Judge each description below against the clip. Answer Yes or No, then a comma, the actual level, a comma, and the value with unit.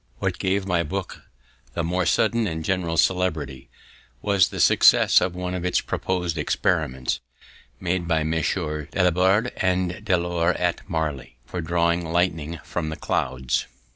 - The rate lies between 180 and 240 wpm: No, average, 145 wpm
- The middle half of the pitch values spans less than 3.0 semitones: Yes, narrow, 2.4 semitones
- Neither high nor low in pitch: No, very low, 85 Hz